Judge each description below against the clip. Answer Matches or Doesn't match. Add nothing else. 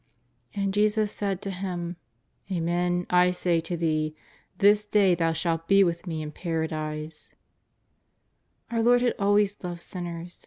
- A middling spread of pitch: Matches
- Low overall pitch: Doesn't match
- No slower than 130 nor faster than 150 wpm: Matches